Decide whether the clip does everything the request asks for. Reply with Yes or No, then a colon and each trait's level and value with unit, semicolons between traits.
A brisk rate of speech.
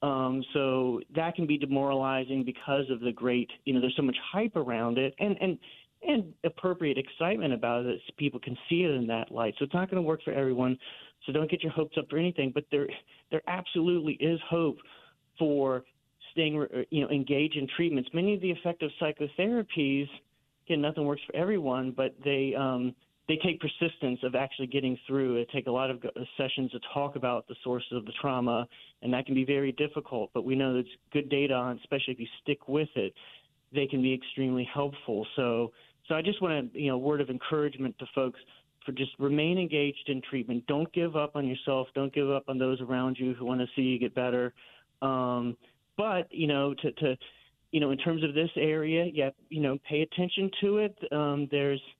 Yes: fast, 210 wpm